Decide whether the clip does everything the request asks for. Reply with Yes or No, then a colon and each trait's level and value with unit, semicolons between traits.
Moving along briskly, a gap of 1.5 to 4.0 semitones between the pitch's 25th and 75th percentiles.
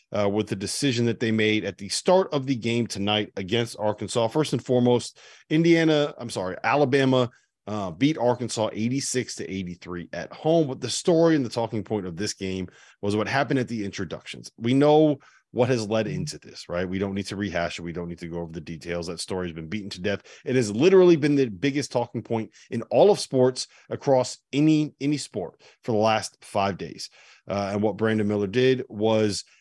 No: fast, 210 wpm; average, 4.8 semitones